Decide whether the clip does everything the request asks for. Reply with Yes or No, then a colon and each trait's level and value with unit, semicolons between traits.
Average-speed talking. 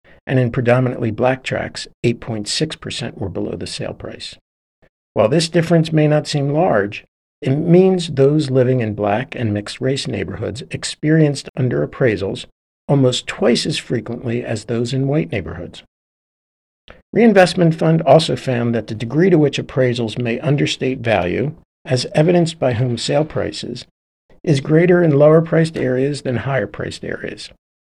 Yes: average, 150 wpm